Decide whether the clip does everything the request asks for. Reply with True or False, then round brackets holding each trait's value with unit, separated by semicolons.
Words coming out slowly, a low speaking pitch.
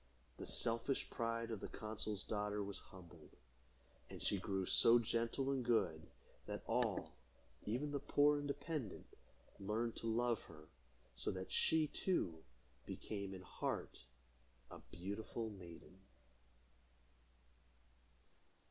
True (120 wpm; 110 Hz)